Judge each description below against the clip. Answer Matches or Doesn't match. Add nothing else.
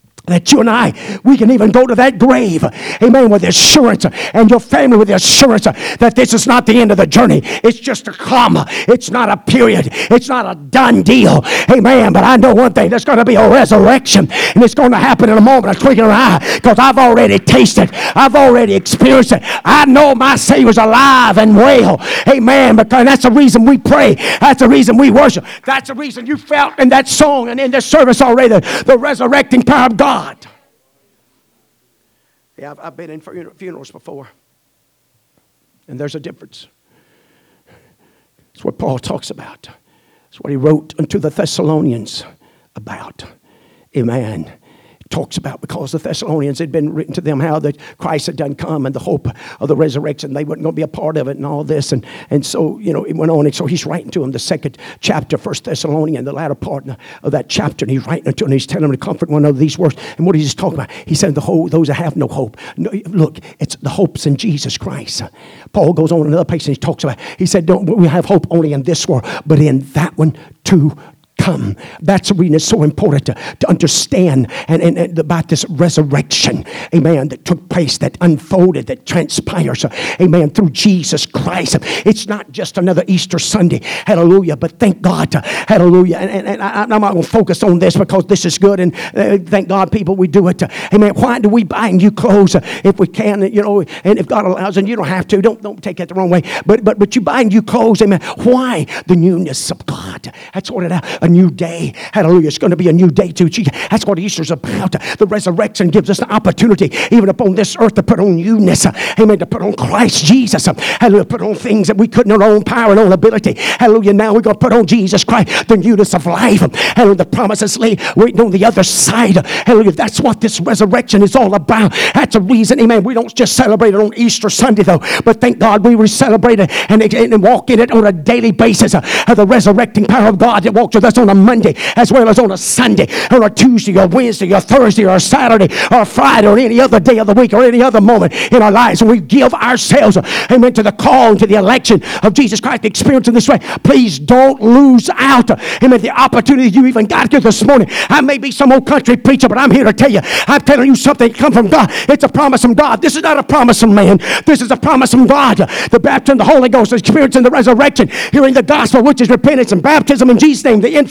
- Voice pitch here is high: Matches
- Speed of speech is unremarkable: Doesn't match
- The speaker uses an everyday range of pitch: Doesn't match